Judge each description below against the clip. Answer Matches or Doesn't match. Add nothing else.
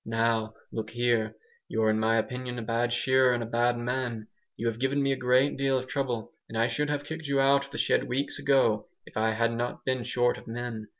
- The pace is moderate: Doesn't match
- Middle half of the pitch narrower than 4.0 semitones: Matches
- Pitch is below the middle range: Matches